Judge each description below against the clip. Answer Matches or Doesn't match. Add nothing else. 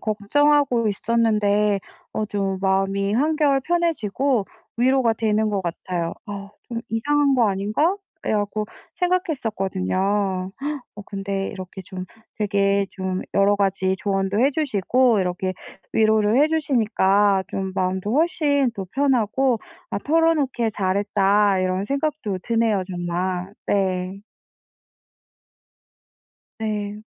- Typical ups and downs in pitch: Matches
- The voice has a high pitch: Matches